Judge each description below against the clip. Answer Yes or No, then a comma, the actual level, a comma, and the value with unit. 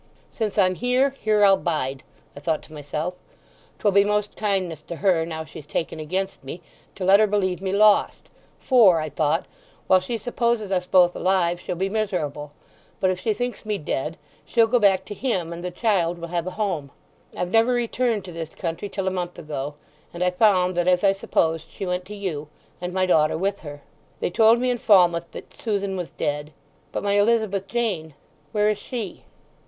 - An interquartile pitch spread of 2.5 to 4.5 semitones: Yes, average, 3.9 semitones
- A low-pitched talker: No, medium, 185 Hz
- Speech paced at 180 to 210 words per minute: Yes, average, 200 wpm